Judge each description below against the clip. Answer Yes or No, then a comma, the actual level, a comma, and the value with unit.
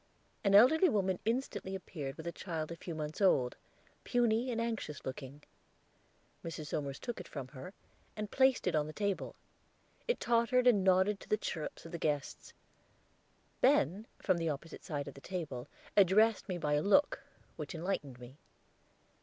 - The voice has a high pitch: No, medium, 180 Hz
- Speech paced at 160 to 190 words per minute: Yes, average, 170 wpm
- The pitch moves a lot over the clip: Yes, wide, 6.2 semitones